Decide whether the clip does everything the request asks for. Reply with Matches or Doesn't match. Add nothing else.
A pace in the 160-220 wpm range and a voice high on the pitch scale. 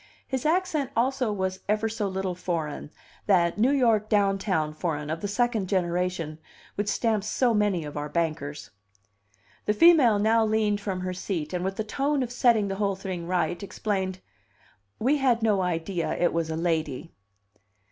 Matches